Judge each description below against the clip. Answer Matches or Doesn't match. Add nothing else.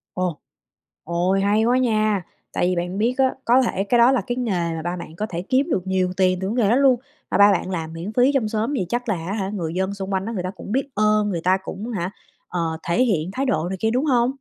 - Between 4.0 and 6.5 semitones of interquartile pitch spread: Matches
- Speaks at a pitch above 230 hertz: Doesn't match